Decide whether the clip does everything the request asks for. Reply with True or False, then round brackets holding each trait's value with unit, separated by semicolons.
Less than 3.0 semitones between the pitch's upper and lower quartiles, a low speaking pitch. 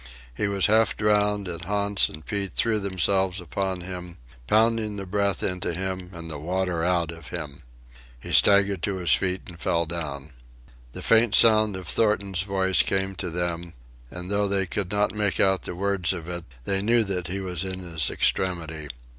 True (2.6 semitones; 95 Hz)